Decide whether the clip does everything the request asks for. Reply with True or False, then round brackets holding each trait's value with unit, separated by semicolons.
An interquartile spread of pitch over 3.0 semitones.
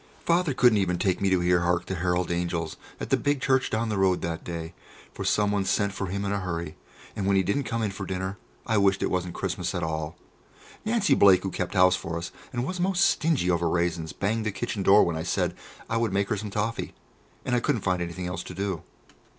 True (3.5 semitones)